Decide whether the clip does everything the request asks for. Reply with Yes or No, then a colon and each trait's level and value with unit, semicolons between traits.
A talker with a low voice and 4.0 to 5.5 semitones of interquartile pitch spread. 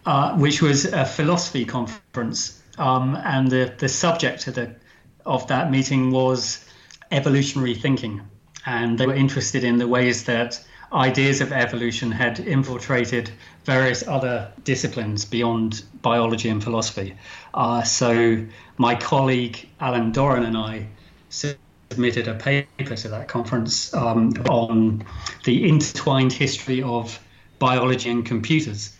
No: low, 125 Hz; average, 2.7 semitones